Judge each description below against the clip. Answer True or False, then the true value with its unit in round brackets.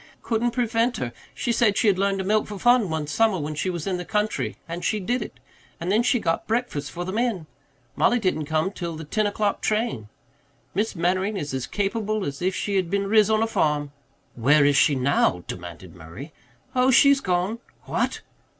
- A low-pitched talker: False (190 Hz)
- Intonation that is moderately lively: False (6.2 semitones)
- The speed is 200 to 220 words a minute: True (205 wpm)